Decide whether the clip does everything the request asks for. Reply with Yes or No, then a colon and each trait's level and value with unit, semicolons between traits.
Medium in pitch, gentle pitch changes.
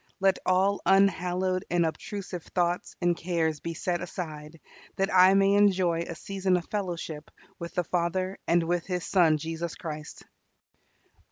Yes: medium, 175 Hz; narrow, 2.1 semitones